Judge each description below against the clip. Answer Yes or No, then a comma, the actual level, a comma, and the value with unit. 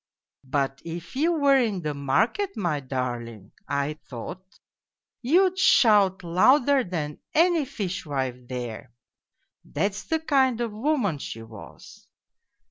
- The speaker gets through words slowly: Yes, slow, 120 wpm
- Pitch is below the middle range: No, medium, 185 Hz